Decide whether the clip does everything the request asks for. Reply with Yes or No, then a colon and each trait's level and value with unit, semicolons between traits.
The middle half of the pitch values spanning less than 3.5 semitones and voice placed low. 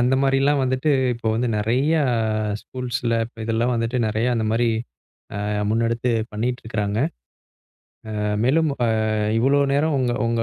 Yes: narrow, 2.4 semitones; low, 120 Hz